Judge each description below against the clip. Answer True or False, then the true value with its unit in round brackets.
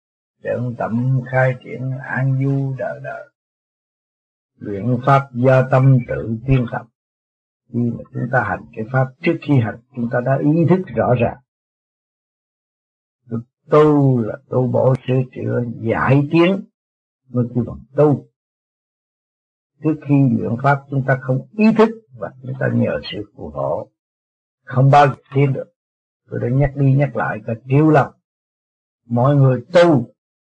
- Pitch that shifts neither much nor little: True (3.1 semitones)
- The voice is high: False (130 Hz)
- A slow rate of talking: True (150 wpm)